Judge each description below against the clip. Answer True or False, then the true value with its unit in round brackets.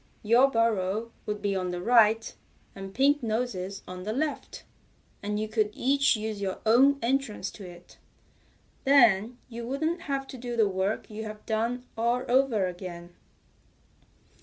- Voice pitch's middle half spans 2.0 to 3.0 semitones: False (3.9 semitones)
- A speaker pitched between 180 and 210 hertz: False (220 Hz)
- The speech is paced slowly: False (150 wpm)